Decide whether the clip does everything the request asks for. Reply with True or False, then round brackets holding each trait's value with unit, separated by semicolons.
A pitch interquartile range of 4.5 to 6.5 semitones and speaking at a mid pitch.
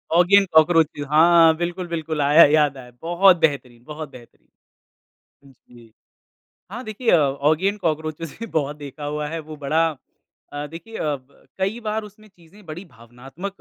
False (3.4 semitones; 155 Hz)